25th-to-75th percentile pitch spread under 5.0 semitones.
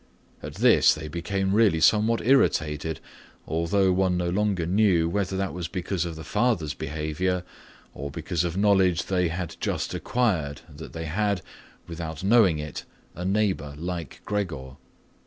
Yes: average, 3.7 semitones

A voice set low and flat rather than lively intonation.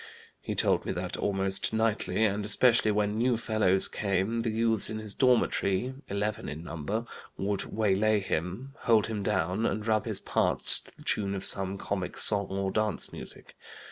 Yes: low, 105 Hz; narrow, 2.3 semitones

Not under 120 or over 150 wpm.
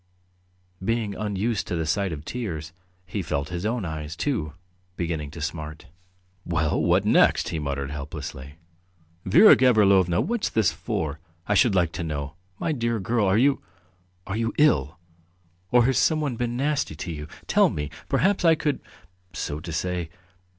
No: average, 160 wpm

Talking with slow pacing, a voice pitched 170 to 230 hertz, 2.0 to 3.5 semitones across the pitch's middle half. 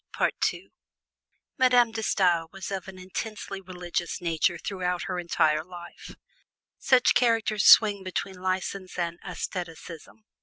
Yes: slow, 115 wpm; medium, 185 Hz; average, 2.8 semitones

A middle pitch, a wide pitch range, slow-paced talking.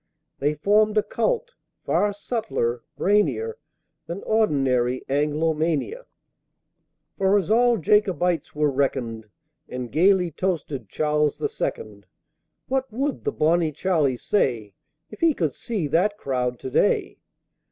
Yes: medium, 165 Hz; wide, 7.4 semitones; slow, 120 wpm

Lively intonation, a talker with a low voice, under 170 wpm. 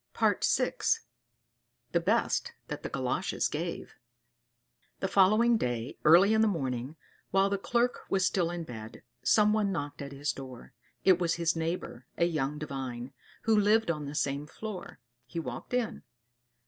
No: wide, 6.4 semitones; medium, 170 Hz; average, 150 wpm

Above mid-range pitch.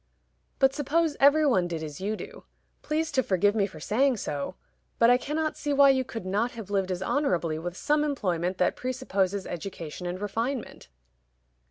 Yes: high, 210 Hz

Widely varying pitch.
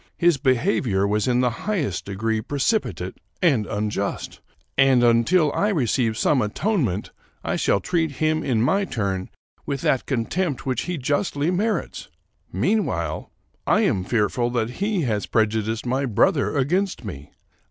Yes: wide, 6.8 semitones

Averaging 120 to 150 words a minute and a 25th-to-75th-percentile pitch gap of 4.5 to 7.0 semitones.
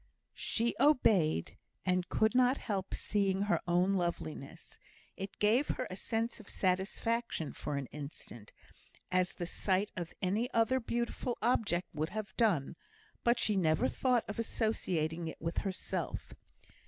Yes: average, 140 wpm; average, 4.9 semitones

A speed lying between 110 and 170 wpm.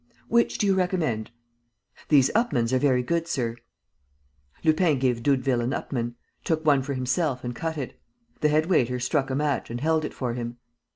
No: average, 180 wpm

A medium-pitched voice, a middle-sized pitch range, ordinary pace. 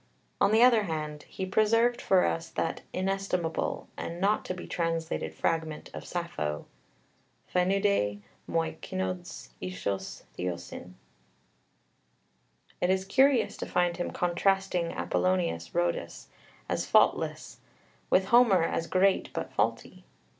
No: medium, 180 Hz; average, 3.4 semitones; slow, 120 wpm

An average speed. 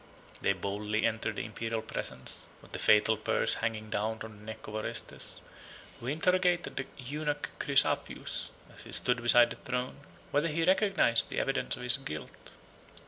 Yes: average, 165 wpm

